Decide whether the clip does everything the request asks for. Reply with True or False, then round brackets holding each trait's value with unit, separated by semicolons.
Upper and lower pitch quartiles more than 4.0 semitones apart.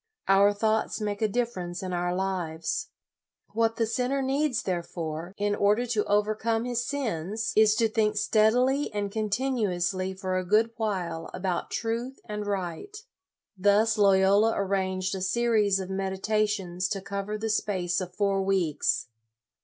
False (3.0 semitones)